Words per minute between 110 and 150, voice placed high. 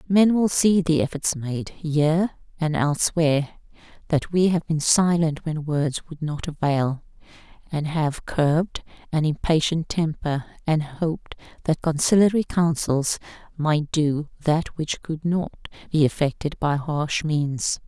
No: average, 140 wpm; medium, 155 Hz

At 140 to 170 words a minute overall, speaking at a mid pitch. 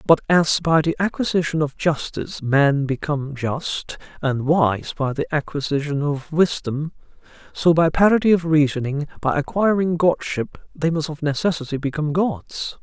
Yes: average, 145 wpm; medium, 155 Hz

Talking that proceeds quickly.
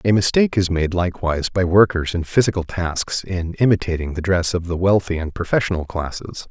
No: average, 185 wpm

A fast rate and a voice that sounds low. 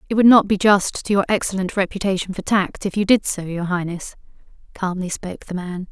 No: fast, 215 wpm; high, 190 Hz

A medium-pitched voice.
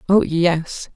Yes: medium, 170 Hz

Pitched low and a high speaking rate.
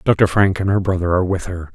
Yes: very low, 90 Hz; fast, 275 wpm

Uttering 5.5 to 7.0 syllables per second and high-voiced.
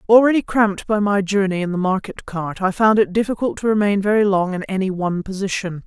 Yes: 6.0 syllables/s; high, 200 Hz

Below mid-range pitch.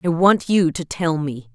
No: medium, 165 Hz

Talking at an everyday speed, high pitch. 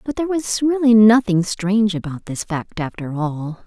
Yes: average, 180 wpm; high, 205 Hz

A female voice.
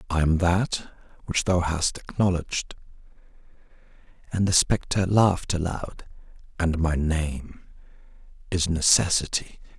No: male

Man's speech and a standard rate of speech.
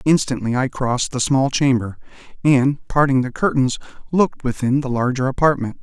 Yes: male; average, 155 wpm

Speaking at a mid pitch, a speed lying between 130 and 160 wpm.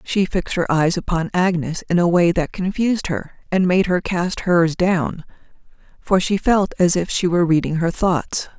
No: medium, 175 Hz; average, 195 wpm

